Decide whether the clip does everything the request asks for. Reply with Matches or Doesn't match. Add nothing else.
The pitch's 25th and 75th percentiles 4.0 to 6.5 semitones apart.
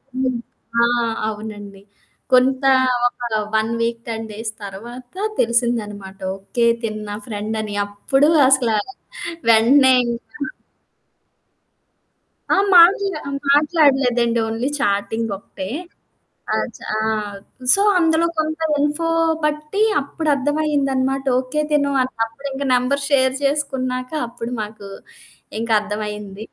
Matches